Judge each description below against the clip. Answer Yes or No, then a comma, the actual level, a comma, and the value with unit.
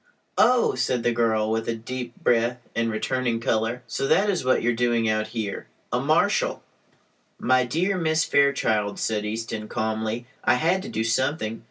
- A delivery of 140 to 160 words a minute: No, average, 175 wpm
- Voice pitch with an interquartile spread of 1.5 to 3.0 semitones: Yes, average, 2.7 semitones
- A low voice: Yes, low, 115 Hz